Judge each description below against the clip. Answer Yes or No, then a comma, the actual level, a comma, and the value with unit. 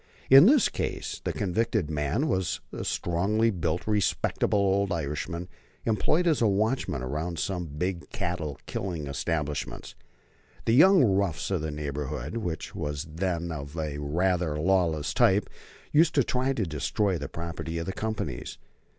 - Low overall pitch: Yes, very low, 85 Hz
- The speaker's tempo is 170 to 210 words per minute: No, average, 150 wpm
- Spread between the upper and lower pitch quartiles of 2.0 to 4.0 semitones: No, wide, 5.5 semitones